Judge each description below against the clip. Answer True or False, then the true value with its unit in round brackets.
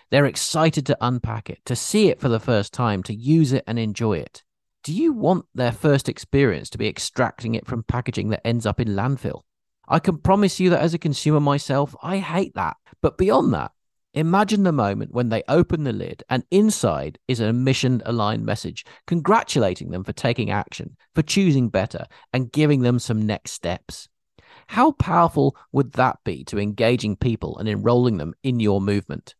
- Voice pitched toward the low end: True (125 Hz)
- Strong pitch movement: True (5.7 semitones)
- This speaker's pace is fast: False (190 wpm)